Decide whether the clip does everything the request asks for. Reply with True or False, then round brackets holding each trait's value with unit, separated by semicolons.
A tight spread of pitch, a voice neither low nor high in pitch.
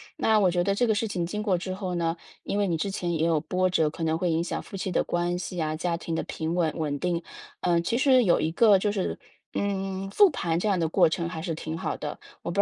False (3.1 semitones; 175 Hz)